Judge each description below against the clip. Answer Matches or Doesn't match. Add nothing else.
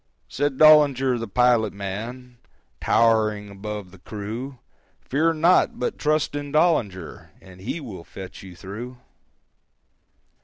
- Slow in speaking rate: Matches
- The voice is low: Matches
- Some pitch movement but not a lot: Doesn't match